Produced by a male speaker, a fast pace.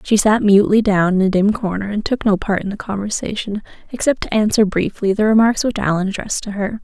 No: female; fast, 230 wpm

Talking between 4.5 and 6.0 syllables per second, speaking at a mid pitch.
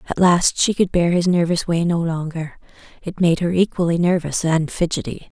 Yes: 5.1 syllables/s; medium, 170 Hz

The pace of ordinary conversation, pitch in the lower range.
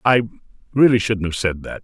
Yes: average, 195 wpm; low, 110 Hz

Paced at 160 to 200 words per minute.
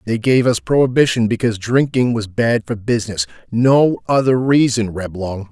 No: average, 150 wpm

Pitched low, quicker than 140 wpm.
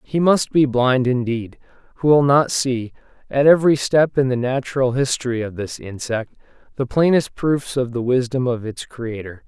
Yes: low, 130 Hz; average, 175 wpm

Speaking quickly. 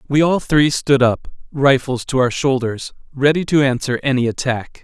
No: average, 175 wpm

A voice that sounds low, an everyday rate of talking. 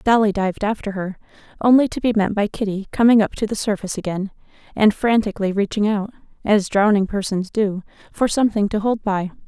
No: high, 205 Hz; average, 185 wpm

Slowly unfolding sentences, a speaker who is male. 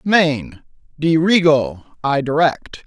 Yes: slow, 65 wpm; male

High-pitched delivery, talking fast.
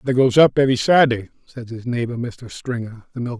No: low, 120 Hz; fast, 210 wpm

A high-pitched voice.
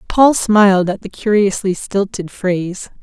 Yes: high, 200 Hz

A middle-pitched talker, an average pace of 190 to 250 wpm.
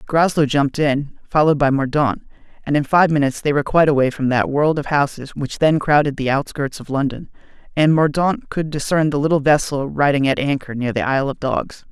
Yes: medium, 145 Hz; fast, 205 wpm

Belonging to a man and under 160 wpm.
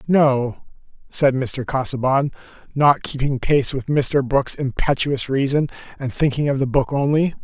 Yes: male; average, 145 wpm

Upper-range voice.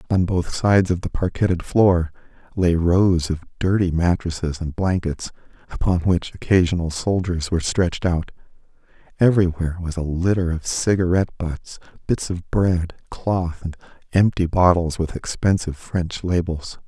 No: very low, 90 Hz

